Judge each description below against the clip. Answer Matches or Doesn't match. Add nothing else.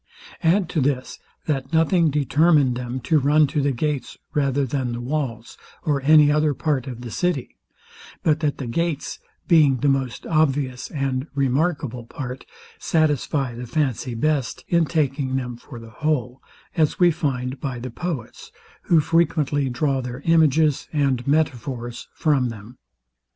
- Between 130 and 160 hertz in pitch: Matches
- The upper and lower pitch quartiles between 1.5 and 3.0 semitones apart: Doesn't match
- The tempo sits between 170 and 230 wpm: Doesn't match